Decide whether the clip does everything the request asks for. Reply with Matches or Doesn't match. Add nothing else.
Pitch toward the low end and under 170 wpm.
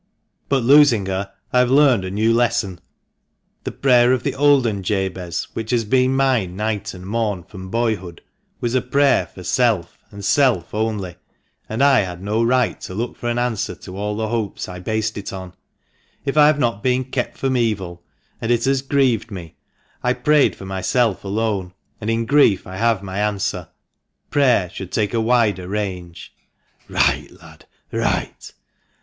Doesn't match